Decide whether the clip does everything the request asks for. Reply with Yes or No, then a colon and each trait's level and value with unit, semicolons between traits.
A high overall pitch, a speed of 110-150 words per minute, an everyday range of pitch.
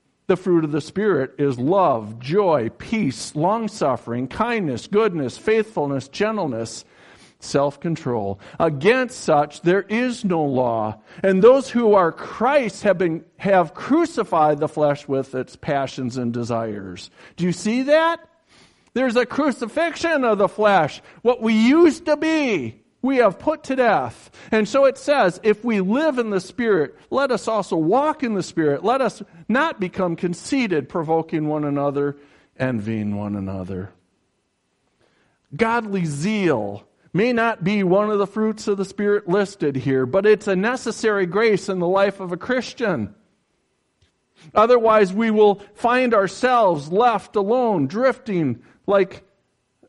No: high, 195 Hz; average, 145 wpm; wide, 7.8 semitones